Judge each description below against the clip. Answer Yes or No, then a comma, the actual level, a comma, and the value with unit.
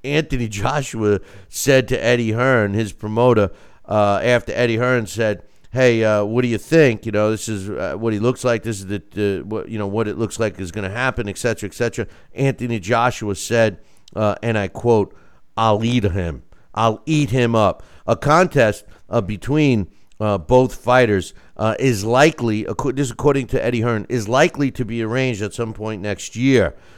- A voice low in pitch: Yes, low, 115 Hz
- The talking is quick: No, average, 195 wpm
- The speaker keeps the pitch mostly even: No, average, 3.2 semitones